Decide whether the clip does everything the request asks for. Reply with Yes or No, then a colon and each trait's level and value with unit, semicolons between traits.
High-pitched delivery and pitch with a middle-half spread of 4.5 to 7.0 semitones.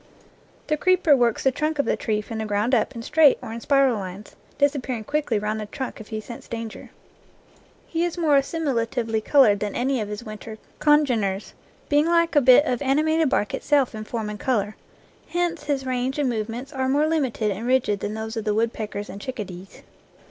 Yes: high, 245 Hz; average, 5.1 semitones